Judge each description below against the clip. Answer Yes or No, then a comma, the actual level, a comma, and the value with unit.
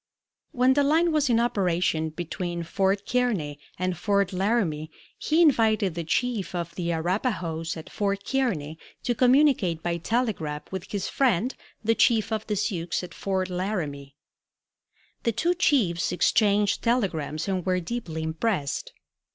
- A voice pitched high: Yes, high, 195 Hz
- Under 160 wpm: Yes, average, 145 wpm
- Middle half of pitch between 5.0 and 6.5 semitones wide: Yes, wide, 5.6 semitones